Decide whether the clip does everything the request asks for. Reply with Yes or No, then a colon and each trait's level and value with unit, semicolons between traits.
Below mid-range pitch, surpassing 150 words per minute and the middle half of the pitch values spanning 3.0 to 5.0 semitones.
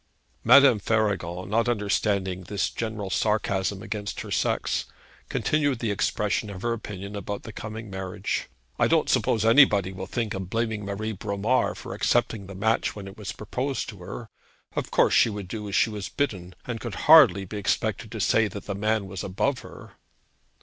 No: low, 105 Hz; average, 180 wpm; narrow, 2.5 semitones